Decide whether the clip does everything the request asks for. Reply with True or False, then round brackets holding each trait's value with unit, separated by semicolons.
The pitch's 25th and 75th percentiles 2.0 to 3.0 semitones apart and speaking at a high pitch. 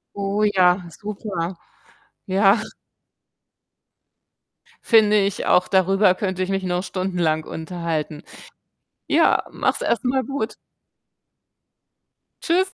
True (2.6 semitones; 195 Hz)